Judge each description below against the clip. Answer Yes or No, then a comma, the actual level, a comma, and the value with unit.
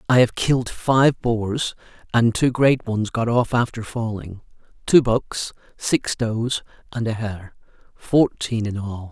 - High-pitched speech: No, low, 115 Hz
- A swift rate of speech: No, average, 150 wpm